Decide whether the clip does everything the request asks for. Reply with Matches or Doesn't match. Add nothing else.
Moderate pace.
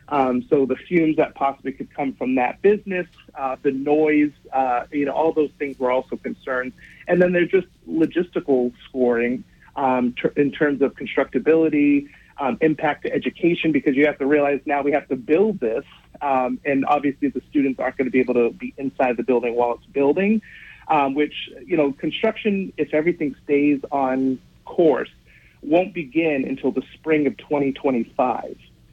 Matches